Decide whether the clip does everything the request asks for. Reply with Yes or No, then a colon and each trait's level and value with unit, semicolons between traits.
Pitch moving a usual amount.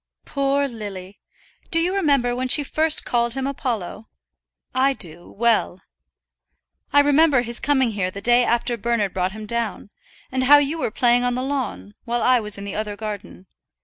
Yes: average, 4.5 semitones